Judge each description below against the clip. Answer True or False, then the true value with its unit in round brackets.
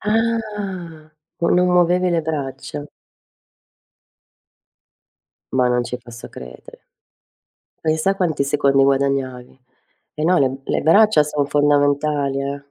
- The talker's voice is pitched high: False (145 Hz)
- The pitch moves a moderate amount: True (4.3 semitones)